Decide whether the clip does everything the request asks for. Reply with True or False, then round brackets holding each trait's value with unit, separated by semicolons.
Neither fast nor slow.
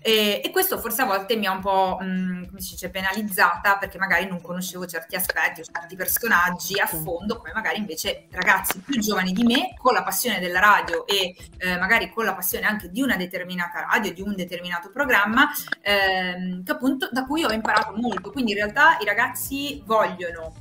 False (200 wpm)